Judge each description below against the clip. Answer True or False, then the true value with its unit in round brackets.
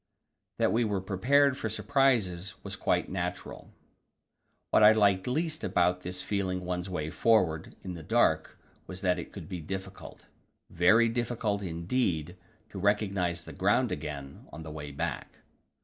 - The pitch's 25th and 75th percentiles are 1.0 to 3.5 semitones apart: False (3.9 semitones)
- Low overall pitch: True (95 Hz)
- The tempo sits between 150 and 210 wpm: True (155 wpm)